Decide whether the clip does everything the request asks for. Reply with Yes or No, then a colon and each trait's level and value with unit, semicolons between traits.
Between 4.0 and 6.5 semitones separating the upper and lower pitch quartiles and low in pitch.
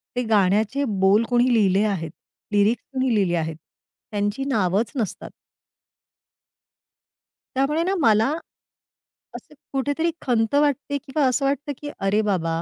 No: average, 5.3 semitones; high, 225 Hz